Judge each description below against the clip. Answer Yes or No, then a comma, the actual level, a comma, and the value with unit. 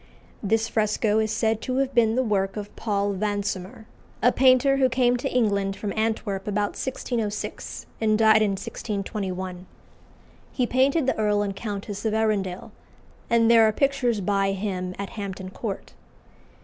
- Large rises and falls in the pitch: No, average, 2.8 semitones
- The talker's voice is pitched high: Yes, high, 215 Hz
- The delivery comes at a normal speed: Yes, average, 155 wpm